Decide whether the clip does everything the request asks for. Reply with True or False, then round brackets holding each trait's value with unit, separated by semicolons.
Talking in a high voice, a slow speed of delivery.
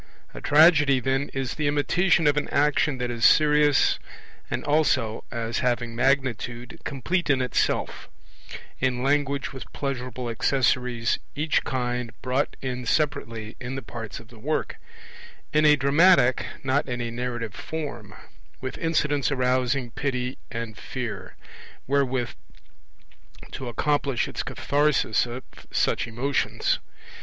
False (130 Hz; 130 wpm)